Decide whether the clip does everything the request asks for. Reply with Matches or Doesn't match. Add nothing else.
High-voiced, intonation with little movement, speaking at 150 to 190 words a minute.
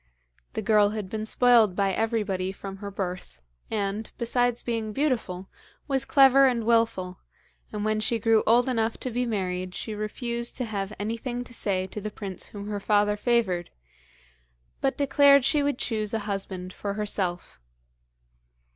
Doesn't match